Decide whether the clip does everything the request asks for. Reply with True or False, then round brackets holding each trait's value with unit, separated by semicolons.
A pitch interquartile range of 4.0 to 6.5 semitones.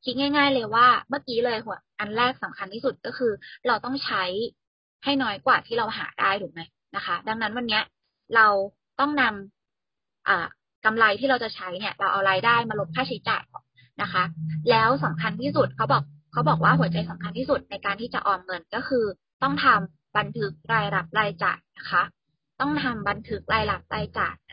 True (5.2 semitones)